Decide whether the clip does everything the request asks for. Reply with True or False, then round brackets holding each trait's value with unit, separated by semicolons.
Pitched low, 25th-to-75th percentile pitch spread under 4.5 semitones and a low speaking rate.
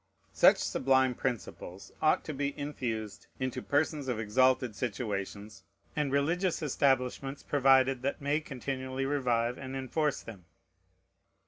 True (130 Hz; 2.8 semitones; 120 wpm)